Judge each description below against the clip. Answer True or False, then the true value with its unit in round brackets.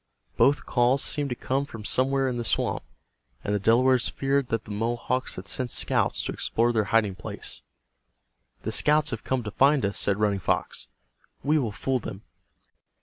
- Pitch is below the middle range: True (120 Hz)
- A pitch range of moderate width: True (4.1 semitones)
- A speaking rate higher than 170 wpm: True (180 wpm)